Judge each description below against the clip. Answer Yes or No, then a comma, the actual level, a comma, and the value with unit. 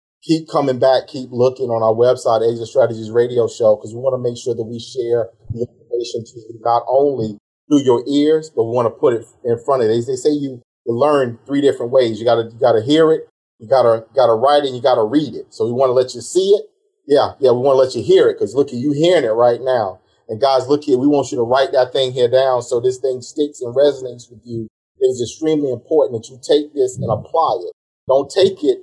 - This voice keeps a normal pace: No, fast, 250 wpm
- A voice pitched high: No, low, 130 Hz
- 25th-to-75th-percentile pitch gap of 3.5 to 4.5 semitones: Yes, average, 4.2 semitones